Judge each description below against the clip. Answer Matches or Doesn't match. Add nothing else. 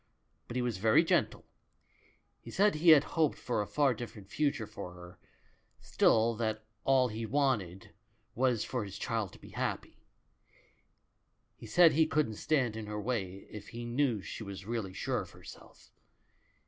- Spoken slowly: Doesn't match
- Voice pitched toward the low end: Matches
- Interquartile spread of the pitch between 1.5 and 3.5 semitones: Doesn't match